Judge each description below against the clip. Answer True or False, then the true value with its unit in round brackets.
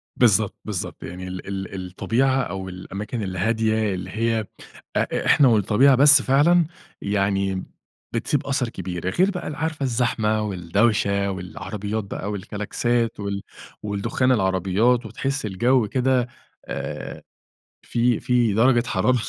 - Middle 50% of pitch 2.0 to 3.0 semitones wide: False (4.2 semitones)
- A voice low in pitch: True (110 Hz)